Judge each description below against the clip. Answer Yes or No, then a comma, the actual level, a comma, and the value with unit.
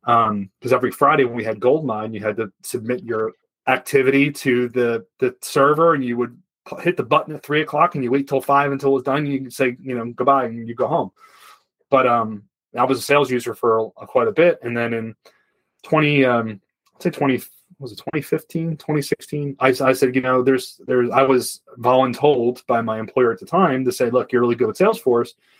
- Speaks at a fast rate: Yes, fast, 220 wpm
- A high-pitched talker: No, low, 130 Hz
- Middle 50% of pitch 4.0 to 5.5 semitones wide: No, average, 2.9 semitones